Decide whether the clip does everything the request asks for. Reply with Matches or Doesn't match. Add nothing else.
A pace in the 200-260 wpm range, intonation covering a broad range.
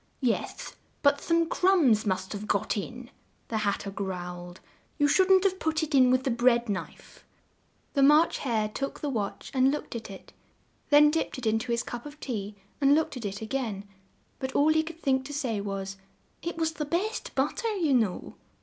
Matches